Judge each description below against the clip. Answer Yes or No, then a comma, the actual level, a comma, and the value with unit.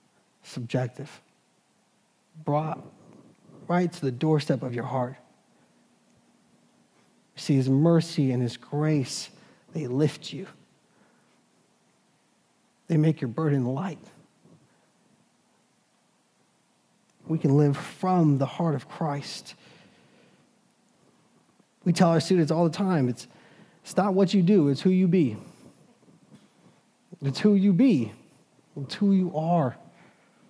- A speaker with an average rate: No, slow, 110 wpm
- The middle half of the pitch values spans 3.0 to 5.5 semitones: Yes, average, 5.1 semitones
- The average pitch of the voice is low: No, medium, 160 Hz